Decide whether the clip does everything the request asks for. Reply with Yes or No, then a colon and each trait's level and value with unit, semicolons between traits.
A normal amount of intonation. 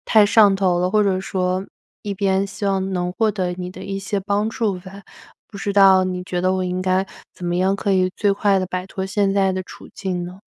No: narrow, 1.4 semitones